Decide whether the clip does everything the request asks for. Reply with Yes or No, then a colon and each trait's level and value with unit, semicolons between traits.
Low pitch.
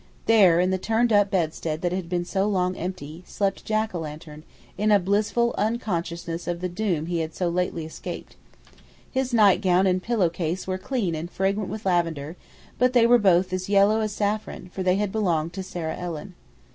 No: medium, 185 Hz